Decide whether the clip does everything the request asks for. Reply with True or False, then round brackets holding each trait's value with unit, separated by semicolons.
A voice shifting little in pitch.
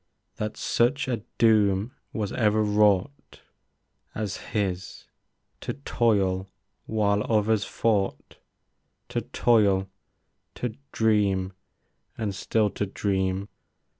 True (2.3 semitones)